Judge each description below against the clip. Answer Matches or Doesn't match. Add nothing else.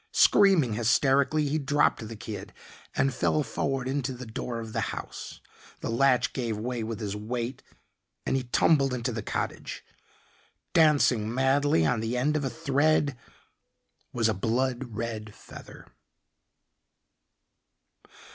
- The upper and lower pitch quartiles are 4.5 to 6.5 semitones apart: Doesn't match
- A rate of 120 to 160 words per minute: Matches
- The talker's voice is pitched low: Matches